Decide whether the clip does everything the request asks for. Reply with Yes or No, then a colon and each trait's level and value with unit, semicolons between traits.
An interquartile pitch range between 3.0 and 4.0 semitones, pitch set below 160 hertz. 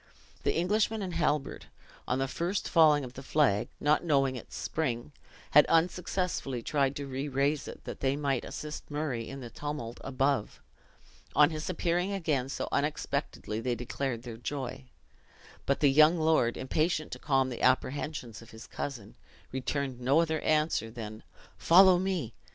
Yes: average, 3.5 semitones; medium, 140 Hz